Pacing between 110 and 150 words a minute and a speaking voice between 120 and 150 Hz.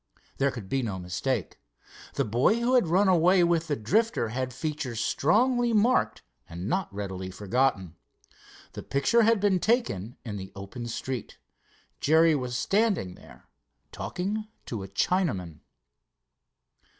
Yes: average, 140 wpm; medium, 140 Hz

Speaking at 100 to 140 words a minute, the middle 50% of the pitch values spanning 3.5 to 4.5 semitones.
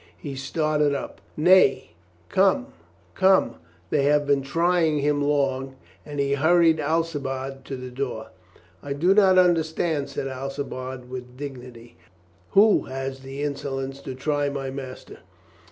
No: slow, 135 wpm; average, 2.9 semitones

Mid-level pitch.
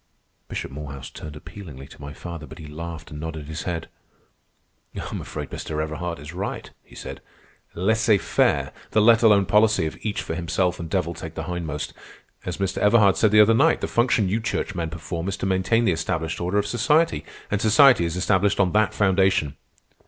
No: very low, 90 Hz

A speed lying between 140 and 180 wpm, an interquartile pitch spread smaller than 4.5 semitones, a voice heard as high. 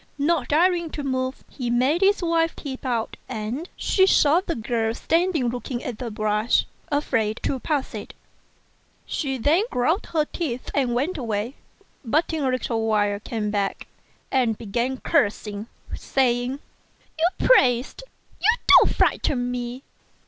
No: average, 145 wpm; average, 4.8 semitones; very high, 255 Hz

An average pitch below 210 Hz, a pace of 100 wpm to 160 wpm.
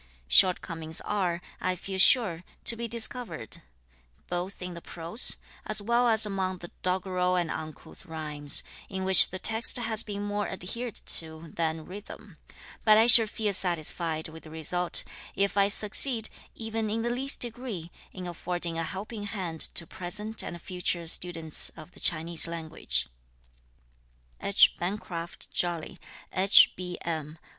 Yes: medium, 185 Hz; average, 145 wpm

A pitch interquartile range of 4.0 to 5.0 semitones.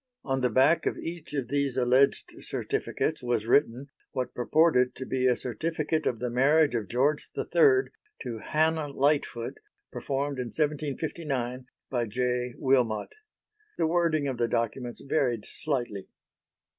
No: average, 3.6 semitones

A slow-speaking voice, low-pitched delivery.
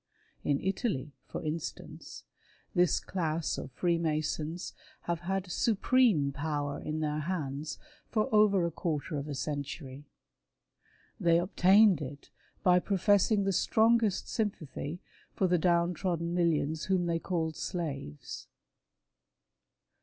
No: slow, 115 wpm; medium, 170 Hz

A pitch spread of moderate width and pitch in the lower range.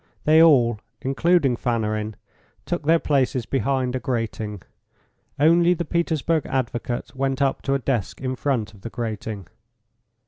Yes: average, 4.4 semitones; low, 130 Hz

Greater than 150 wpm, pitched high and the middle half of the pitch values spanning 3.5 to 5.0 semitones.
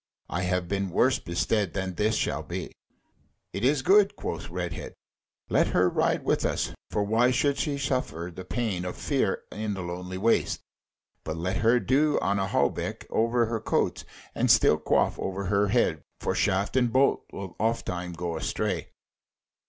No: average, 170 wpm; low, 100 Hz; average, 4.6 semitones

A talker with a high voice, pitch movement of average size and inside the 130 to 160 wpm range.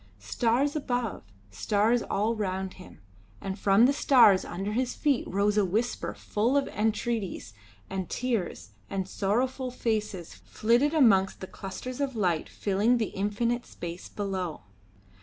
Yes: high, 210 Hz; average, 4.2 semitones; average, 140 wpm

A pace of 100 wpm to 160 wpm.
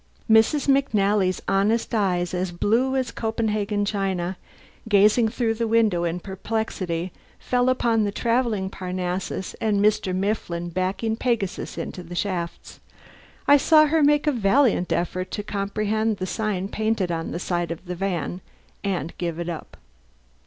Yes: average, 145 wpm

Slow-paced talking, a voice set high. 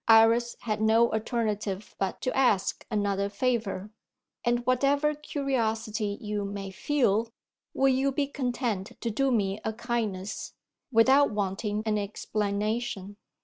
Yes: slow, 125 wpm; high, 220 Hz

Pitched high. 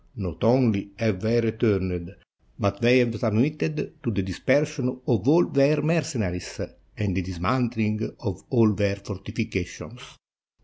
No: low, 110 Hz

